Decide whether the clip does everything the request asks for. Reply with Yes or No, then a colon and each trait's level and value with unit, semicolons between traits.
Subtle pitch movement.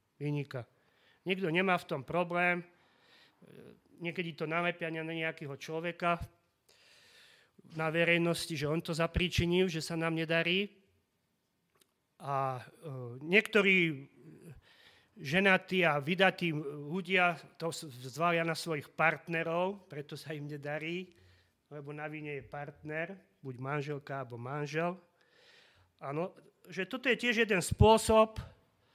No: average, 3.4 semitones